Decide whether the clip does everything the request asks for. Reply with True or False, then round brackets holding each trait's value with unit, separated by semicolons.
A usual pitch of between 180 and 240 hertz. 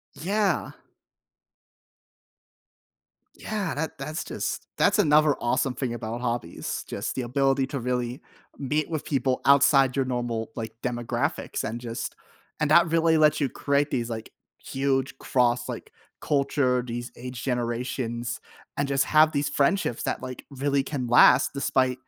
False (130 Hz)